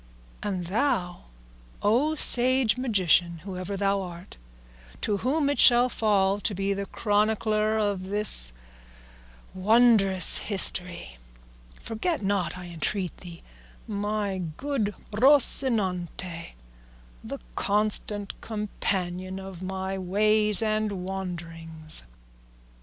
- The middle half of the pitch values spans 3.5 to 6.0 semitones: No, average, 2.9 semitones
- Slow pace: Yes, slow, 95 wpm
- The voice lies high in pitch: Yes, high, 200 Hz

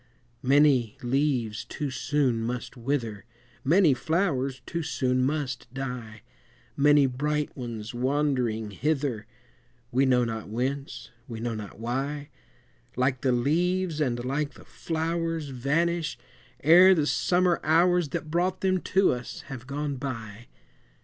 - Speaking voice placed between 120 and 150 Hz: Yes, low, 135 Hz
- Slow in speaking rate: Yes, slow, 130 wpm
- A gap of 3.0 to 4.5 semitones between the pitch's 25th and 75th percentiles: Yes, average, 4.1 semitones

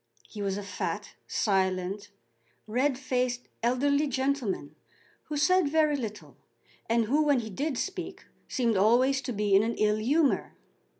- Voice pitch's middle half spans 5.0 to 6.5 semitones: Yes, average, 5.3 semitones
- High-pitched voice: Yes, high, 245 Hz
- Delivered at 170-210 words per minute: No, average, 145 wpm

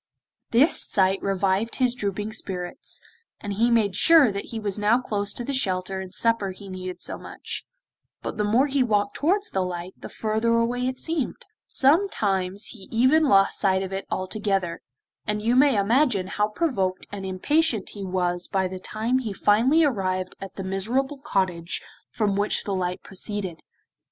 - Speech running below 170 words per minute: No, average, 175 wpm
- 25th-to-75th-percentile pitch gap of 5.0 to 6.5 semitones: No, average, 4.2 semitones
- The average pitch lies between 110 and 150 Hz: No, high, 205 Hz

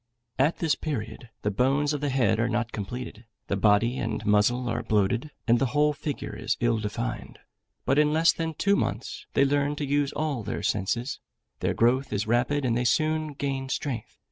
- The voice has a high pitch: No, low, 130 Hz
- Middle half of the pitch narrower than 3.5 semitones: No, average, 4.1 semitones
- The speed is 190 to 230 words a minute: Yes, average, 195 wpm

